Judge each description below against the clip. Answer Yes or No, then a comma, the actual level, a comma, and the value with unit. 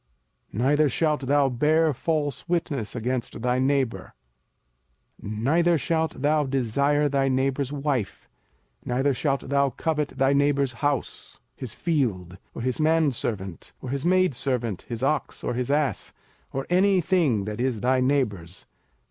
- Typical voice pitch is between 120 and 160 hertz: Yes, low, 135 Hz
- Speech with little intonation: No, average, 3.3 semitones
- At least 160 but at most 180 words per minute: No, average, 140 wpm